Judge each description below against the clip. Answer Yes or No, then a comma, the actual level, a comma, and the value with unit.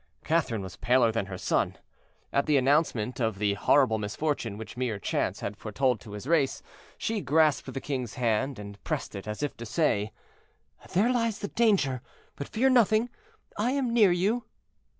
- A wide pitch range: Yes, wide, 8.8 semitones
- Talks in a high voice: No, low, 135 Hz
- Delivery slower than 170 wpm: No, average, 175 wpm